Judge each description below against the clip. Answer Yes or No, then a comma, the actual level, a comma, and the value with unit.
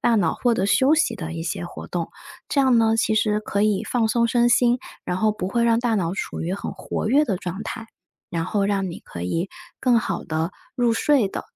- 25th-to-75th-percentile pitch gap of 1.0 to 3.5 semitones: No, average, 4.5 semitones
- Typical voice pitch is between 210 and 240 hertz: Yes, high, 215 Hz